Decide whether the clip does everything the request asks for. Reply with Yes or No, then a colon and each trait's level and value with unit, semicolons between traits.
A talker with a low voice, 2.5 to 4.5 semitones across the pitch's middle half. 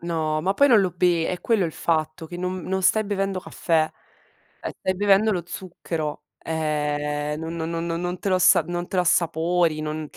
No: medium, 170 Hz; average, 2.8 semitones